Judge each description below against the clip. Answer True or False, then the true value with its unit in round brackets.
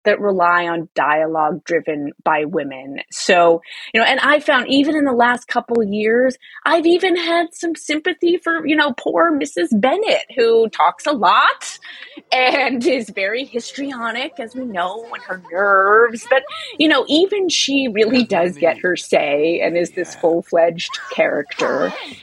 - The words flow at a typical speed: True (160 wpm)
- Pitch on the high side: True (240 Hz)